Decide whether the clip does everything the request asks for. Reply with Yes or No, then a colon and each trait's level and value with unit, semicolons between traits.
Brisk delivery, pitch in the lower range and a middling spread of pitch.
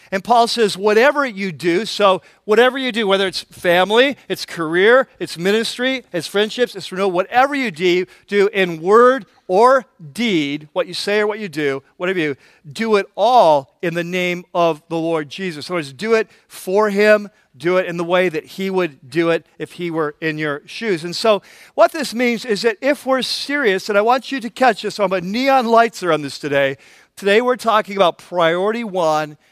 No: fast, 210 wpm; high, 195 Hz; average, 4.8 semitones